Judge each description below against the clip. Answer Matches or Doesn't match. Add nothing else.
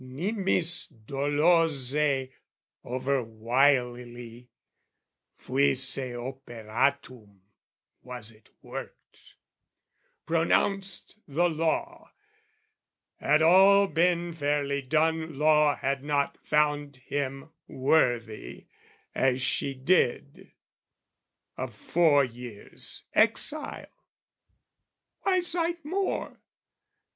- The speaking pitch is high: Doesn't match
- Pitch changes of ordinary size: Matches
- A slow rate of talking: Matches